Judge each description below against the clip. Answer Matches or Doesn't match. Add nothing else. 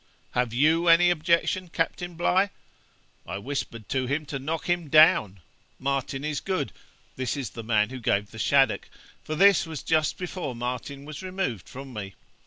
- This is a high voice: Doesn't match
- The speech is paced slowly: Doesn't match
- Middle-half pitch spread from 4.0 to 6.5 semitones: Matches